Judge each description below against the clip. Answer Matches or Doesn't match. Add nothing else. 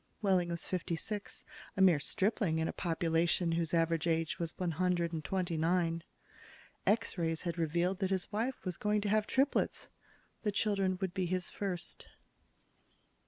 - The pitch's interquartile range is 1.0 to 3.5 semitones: Matches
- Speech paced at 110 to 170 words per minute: Matches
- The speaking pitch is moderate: Matches